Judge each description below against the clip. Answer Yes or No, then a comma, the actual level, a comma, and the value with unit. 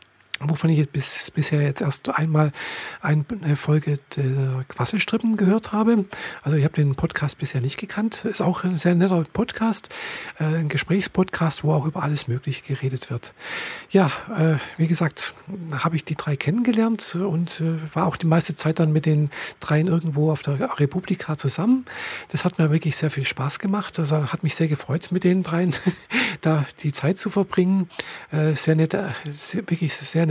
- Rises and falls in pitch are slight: No, average, 3.7 semitones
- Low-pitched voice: No, medium, 160 Hz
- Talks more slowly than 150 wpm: No, average, 170 wpm